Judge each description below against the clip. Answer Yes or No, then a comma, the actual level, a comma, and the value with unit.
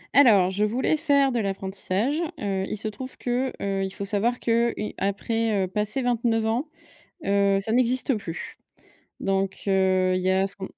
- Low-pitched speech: No, high, 210 Hz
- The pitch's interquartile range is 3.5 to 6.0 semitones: Yes, average, 3.8 semitones